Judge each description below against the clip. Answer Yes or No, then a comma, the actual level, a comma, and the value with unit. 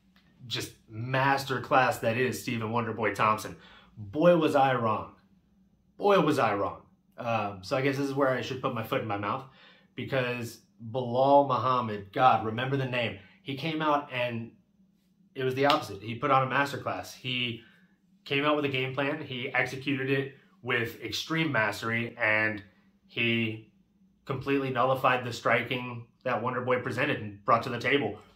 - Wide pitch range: No, average, 3.5 semitones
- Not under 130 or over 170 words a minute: Yes, average, 165 wpm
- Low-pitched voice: Yes, low, 130 Hz